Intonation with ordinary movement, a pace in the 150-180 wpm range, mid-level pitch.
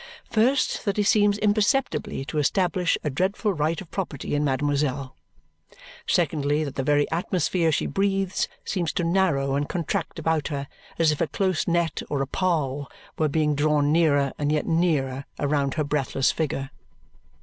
Yes: average, 4.3 semitones; average, 160 wpm; medium, 155 Hz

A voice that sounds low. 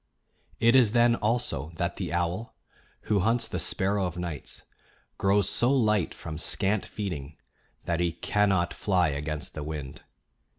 Yes: very low, 95 Hz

